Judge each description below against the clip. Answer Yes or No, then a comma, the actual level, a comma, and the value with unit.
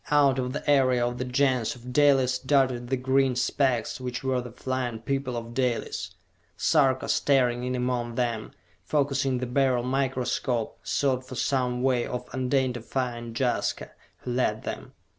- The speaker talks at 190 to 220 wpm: No, average, 155 wpm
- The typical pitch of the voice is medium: No, low, 125 Hz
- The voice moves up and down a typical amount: No, narrow, 1.5 semitones